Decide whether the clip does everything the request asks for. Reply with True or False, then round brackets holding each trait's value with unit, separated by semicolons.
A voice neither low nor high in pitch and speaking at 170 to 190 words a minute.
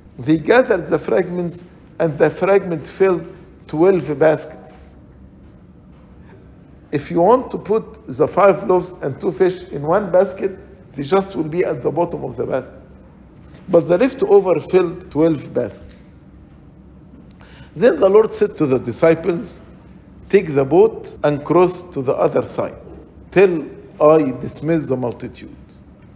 False (175 Hz; 140 wpm)